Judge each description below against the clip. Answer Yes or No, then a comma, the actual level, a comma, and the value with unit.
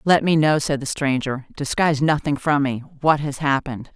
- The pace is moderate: Yes, average, 165 wpm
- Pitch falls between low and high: Yes, medium, 145 Hz